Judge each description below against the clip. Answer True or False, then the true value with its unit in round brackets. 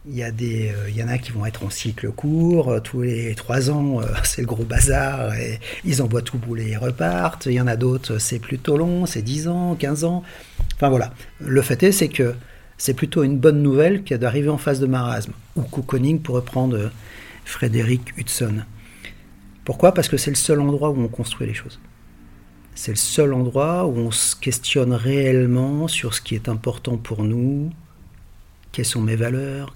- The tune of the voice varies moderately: True (3.6 semitones)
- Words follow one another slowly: False (205 wpm)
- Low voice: True (125 Hz)